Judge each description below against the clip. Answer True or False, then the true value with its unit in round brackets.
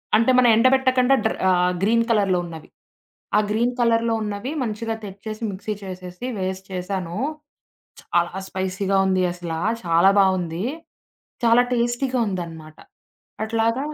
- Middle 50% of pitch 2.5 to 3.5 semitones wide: False (4.1 semitones)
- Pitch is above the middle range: True (200 Hz)